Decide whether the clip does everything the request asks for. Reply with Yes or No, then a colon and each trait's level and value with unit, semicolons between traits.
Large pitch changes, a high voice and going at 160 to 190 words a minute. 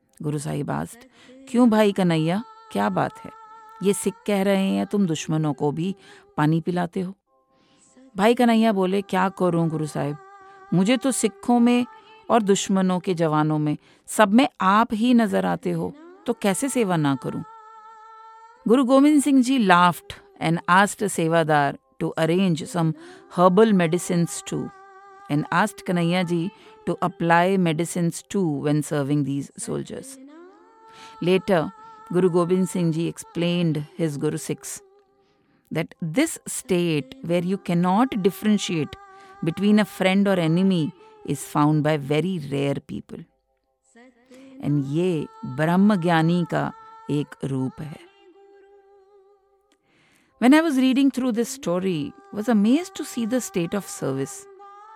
No: wide, 8.0 semitones; high, 195 Hz; slow, 135 wpm